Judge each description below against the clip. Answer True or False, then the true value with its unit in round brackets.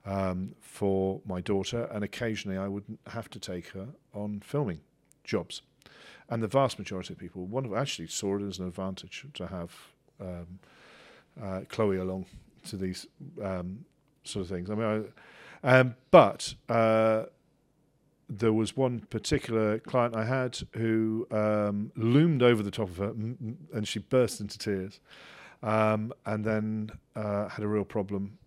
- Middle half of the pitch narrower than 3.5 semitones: True (3.0 semitones)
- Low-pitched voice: True (105 Hz)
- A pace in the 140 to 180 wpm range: True (160 wpm)